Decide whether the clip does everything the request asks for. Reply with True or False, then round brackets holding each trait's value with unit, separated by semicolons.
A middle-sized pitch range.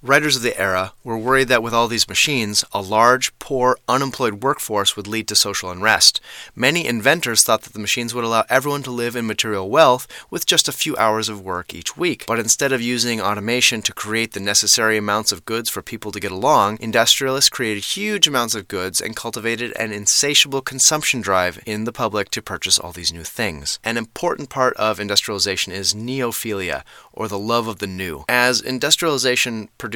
True (3.2 semitones)